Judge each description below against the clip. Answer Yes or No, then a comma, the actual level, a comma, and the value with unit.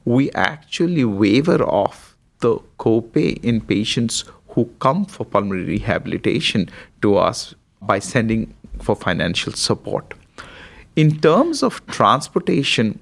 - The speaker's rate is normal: No, slow, 110 wpm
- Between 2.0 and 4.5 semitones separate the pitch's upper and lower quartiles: No, average, 4.9 semitones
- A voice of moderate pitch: No, low, 120 Hz